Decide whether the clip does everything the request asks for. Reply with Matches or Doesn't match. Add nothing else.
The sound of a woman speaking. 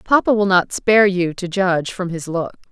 Matches